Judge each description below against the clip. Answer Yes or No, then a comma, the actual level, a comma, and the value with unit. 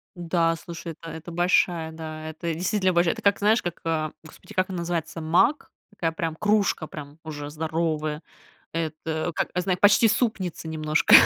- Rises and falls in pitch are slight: Yes, narrow, 2.3 semitones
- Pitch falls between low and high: Yes, medium, 165 Hz